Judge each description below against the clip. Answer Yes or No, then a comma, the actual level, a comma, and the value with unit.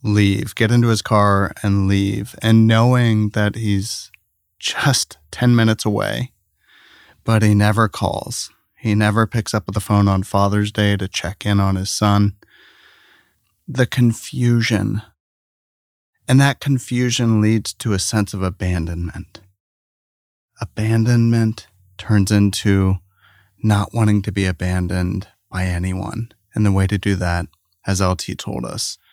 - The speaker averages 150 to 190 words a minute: No, slow, 135 wpm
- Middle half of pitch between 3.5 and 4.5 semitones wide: No, average, 2.8 semitones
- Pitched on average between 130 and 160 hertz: No, low, 105 Hz